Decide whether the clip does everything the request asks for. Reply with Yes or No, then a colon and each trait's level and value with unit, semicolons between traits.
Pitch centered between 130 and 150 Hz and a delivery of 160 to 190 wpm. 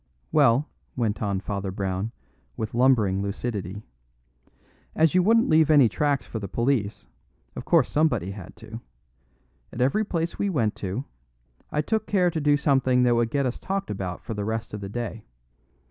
No: low, 120 Hz; average, 175 wpm